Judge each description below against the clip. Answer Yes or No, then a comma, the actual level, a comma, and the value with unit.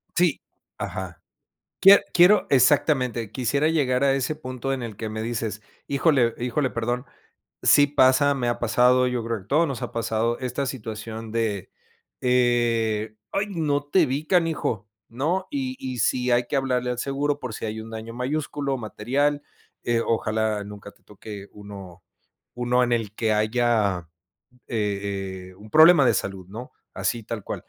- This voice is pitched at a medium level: No, low, 120 Hz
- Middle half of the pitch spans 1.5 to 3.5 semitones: No, average, 4.1 semitones